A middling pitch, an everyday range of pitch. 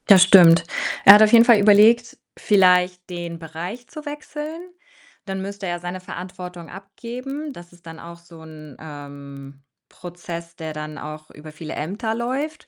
Yes: medium, 180 Hz; average, 4.7 semitones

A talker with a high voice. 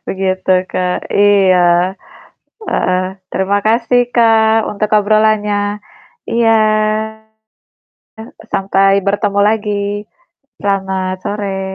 Yes: high, 205 Hz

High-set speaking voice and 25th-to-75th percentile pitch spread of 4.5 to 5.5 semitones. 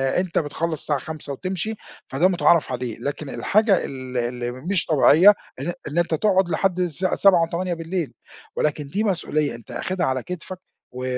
No: medium, 165 Hz; average, 4.8 semitones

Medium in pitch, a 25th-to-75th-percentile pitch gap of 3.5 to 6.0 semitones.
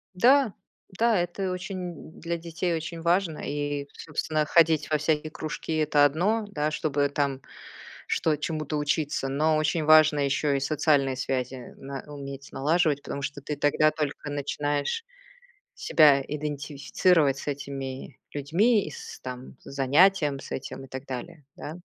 No: medium, 150 Hz; average, 2.7 semitones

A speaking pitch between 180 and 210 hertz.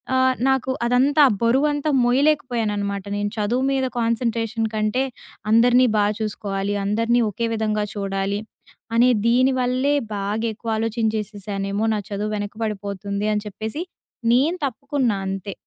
No: high, 220 Hz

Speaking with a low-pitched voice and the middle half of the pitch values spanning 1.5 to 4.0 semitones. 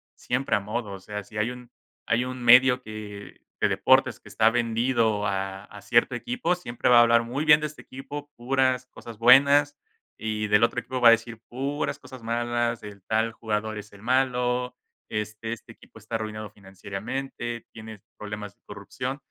Yes: low, 115 Hz; average, 2.9 semitones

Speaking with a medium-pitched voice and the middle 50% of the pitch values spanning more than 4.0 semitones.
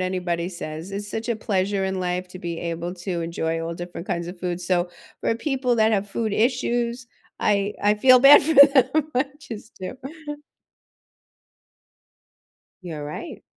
No: high, 195 Hz; average, 5.2 semitones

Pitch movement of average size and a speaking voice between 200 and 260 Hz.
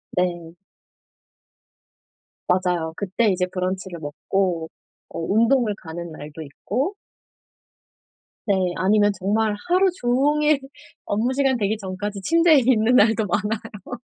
Yes: average, 4.9 semitones; high, 205 Hz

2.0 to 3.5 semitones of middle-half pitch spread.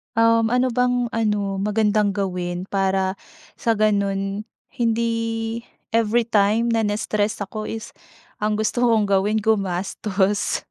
Yes: narrow, 2.4 semitones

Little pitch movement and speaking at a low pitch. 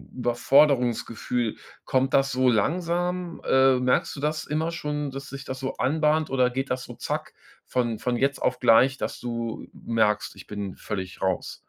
No: average, 3.6 semitones; low, 130 Hz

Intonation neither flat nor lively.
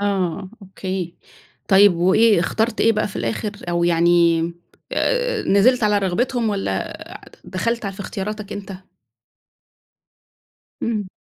Yes: average, 3.7 semitones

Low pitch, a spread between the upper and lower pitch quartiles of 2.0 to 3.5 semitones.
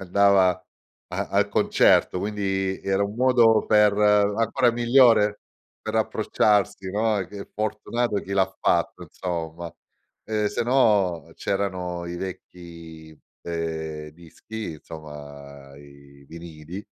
No: very low, 95 Hz; average, 4.3 semitones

